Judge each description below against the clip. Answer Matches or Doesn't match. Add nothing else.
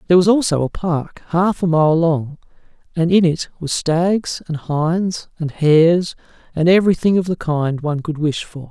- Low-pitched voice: Doesn't match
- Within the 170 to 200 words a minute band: Matches